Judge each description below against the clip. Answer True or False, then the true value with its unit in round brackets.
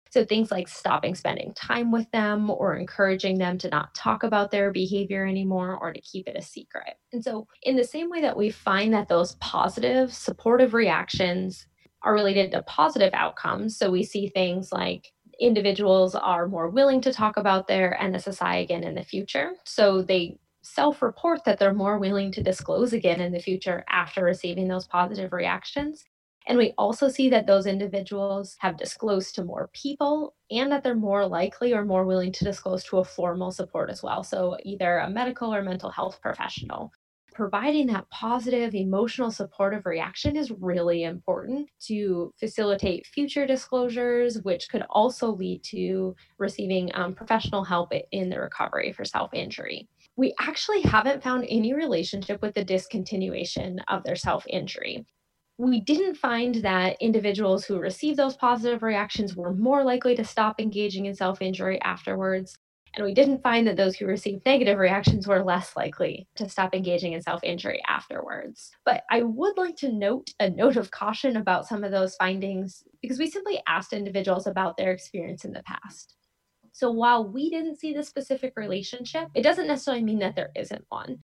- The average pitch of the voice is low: False (200 Hz)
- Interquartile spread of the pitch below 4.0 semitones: False (4.6 semitones)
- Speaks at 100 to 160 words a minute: False (175 wpm)